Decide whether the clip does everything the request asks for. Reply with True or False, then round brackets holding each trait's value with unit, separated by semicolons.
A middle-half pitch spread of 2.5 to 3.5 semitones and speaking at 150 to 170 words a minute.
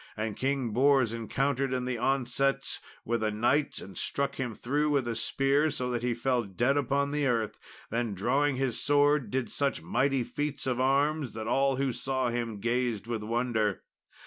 False (2.9 semitones; 185 wpm)